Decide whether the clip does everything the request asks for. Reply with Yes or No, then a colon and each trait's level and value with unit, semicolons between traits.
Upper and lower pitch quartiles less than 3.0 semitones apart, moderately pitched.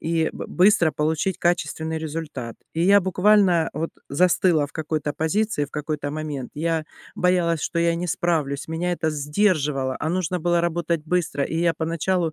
Yes: narrow, 2.5 semitones; medium, 165 Hz